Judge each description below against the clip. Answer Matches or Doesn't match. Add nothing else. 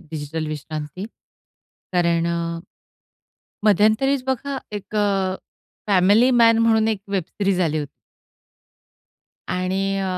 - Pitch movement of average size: Matches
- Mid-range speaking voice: Doesn't match